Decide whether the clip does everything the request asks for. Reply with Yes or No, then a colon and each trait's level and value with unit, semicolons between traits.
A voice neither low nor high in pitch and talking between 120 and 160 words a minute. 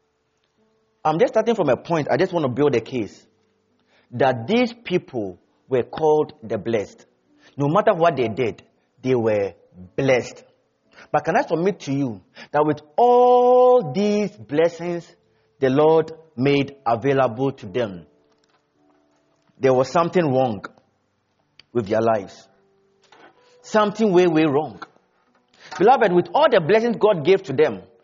Yes: medium, 150 Hz; average, 140 wpm